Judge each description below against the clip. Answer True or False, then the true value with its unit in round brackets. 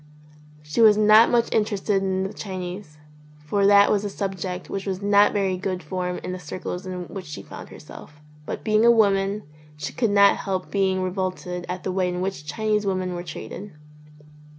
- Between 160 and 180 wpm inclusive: False (190 wpm)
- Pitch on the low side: False (190 Hz)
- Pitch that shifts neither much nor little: False (2.0 semitones)